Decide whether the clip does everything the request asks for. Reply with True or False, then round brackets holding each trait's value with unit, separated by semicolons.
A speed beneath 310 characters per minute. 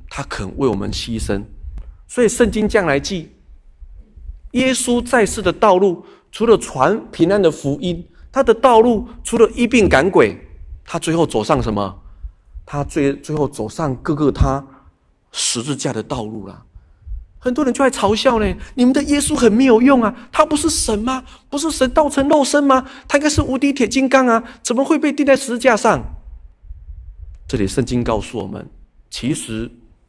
True (245 characters per minute)